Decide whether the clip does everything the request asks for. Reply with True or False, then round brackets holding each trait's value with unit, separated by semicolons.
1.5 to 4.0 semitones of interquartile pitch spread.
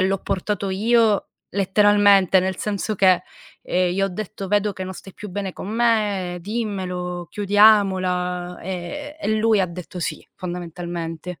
True (2.5 semitones)